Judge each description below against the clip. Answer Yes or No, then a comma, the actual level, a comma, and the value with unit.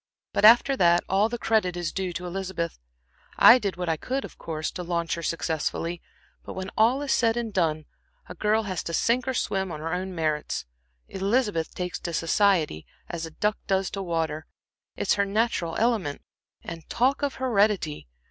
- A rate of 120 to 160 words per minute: No, average, 185 wpm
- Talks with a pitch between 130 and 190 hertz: Yes, medium, 185 Hz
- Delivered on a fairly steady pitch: No, average, 4.7 semitones